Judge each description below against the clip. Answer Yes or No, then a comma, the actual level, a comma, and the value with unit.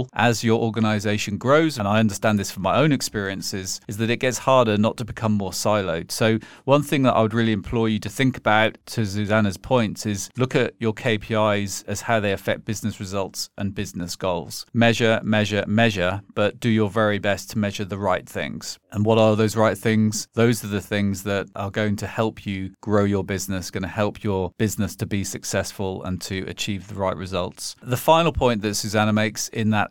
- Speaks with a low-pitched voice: Yes, low, 105 Hz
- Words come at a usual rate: No, fast, 210 wpm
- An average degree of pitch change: No, narrow, 2.2 semitones